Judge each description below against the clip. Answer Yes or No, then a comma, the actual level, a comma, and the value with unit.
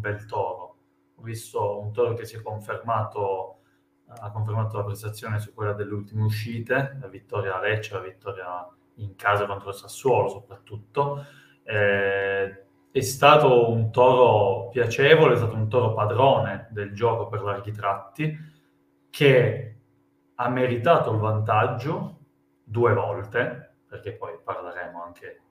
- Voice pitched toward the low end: Yes, low, 105 Hz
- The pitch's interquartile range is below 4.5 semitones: Yes, average, 3.5 semitones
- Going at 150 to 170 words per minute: No, average, 140 wpm